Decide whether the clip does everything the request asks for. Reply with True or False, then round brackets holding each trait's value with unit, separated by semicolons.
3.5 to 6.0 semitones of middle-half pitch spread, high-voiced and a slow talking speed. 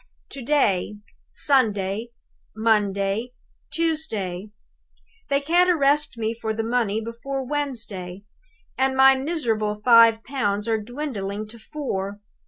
True (4.7 semitones; 230 Hz; 110 wpm)